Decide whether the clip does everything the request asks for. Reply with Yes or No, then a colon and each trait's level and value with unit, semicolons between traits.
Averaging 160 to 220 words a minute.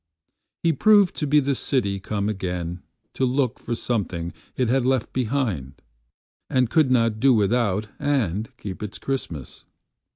No: slow, 135 wpm